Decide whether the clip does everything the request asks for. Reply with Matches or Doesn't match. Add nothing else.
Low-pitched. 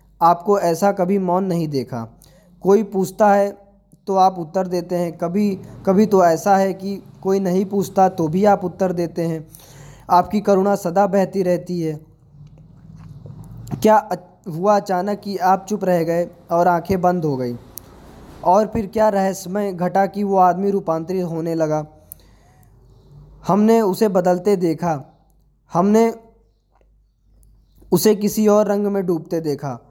Doesn't match